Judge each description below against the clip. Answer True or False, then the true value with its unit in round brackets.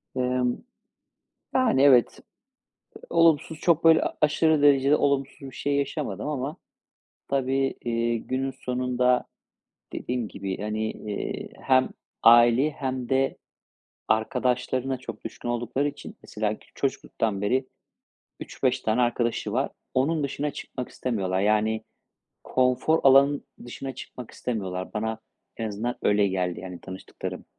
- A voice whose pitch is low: True (125 Hz)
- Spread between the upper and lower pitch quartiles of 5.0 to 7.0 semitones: False (3.7 semitones)